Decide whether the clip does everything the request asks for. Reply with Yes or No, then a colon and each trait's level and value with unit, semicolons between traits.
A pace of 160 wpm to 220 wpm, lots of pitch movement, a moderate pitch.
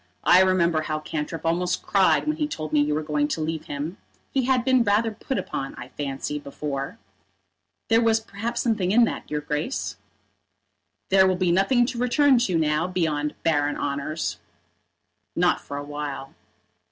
Yes: average, 170 wpm; wide, 7.0 semitones; medium, 170 Hz